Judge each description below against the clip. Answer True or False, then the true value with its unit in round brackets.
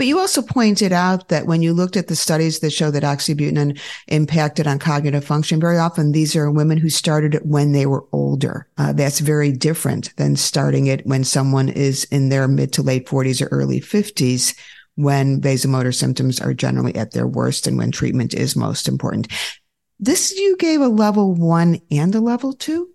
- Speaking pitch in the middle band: True (150 Hz)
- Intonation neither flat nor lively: True (4.0 semitones)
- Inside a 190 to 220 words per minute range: True (195 wpm)